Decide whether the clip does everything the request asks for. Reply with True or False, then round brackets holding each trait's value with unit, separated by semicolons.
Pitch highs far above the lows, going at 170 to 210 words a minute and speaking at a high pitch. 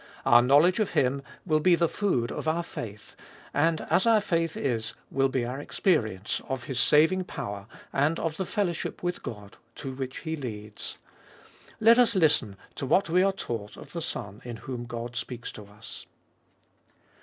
False (6.2 semitones; 180 wpm; 135 Hz)